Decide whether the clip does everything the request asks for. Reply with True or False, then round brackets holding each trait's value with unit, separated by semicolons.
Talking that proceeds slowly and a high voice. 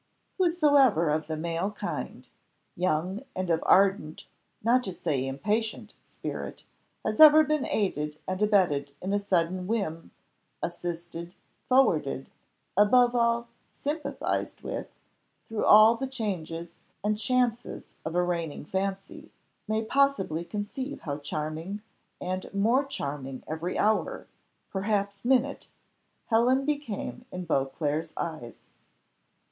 True (115 wpm; 195 Hz)